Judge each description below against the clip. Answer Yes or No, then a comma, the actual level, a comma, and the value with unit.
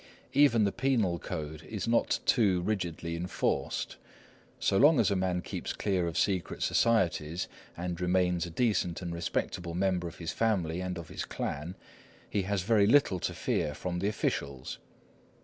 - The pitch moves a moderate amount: Yes, average, 3.4 semitones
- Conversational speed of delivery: Yes, average, 165 wpm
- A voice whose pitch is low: Yes, very low, 90 Hz